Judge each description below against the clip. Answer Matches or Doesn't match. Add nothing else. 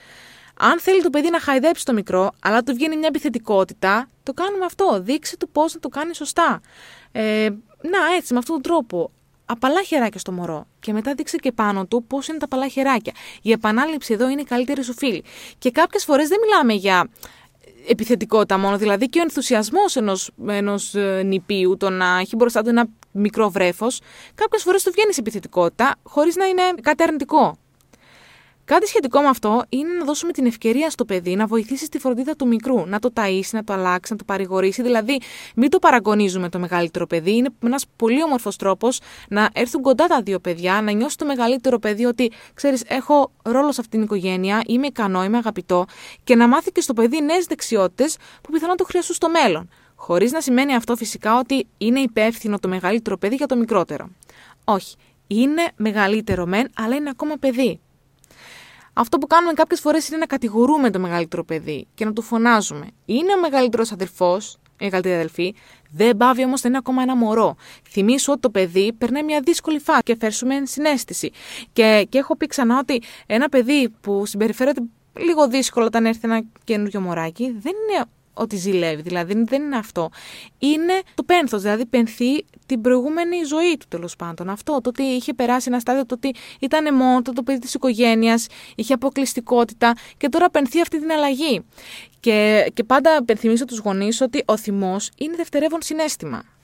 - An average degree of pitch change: Doesn't match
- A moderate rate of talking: Doesn't match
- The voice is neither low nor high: Doesn't match